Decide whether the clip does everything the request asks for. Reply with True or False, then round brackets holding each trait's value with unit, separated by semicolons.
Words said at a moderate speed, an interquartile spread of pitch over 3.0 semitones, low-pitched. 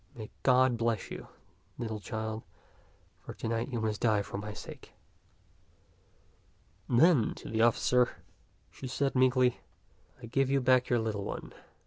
False (150 wpm; 2.6 semitones; 120 Hz)